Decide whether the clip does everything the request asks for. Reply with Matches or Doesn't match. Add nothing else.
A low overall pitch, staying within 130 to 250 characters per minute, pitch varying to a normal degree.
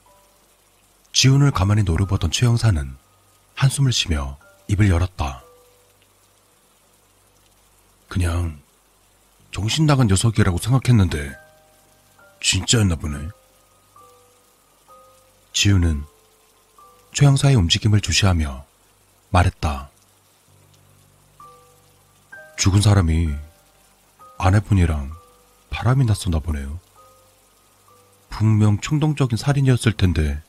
Matches